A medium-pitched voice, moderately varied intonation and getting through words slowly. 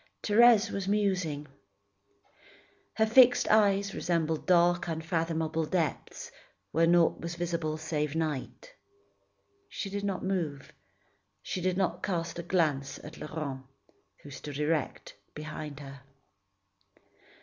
Yes: medium, 165 Hz; average, 3.6 semitones; slow, 115 wpm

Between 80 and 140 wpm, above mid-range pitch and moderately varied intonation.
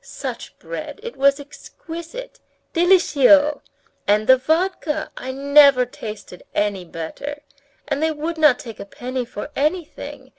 Yes: slow, 135 wpm; very high, 285 Hz; average, 4.1 semitones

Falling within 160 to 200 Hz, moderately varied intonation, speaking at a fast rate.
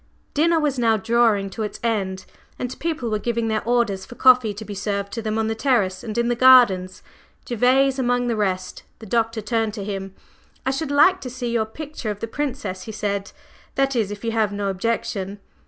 No: high, 225 Hz; average, 3.4 semitones; fast, 210 wpm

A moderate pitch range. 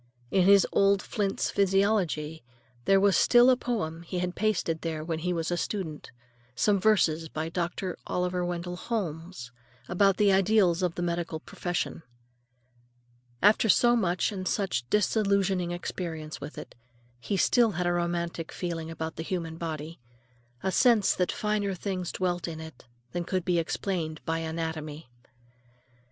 Yes: average, 3.2 semitones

